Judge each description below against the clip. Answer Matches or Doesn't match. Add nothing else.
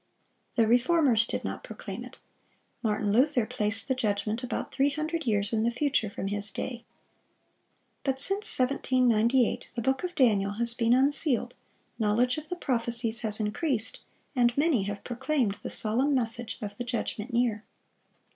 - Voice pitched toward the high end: Matches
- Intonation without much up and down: Doesn't match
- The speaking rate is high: Doesn't match